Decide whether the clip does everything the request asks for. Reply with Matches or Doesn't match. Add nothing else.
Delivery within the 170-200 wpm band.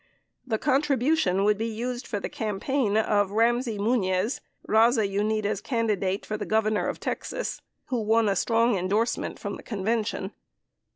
Doesn't match